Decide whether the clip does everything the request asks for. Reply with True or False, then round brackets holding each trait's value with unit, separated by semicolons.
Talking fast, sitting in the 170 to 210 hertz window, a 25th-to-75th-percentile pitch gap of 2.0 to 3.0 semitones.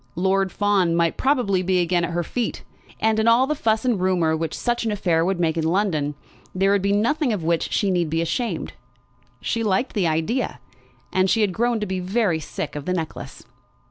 False (210 wpm; 190 Hz; 4.6 semitones)